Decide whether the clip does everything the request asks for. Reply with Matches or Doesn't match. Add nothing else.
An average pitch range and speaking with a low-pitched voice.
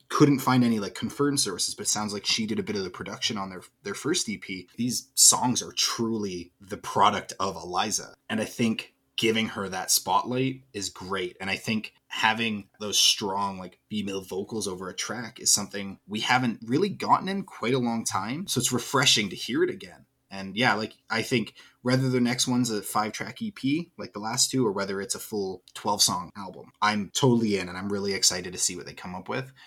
Matches